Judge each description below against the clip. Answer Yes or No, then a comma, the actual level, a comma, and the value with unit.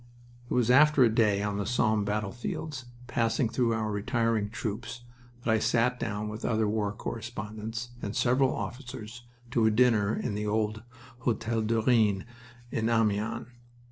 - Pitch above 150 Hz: No, low, 115 Hz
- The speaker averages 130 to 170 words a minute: Yes, average, 155 wpm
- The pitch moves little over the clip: Yes, narrow, 2.1 semitones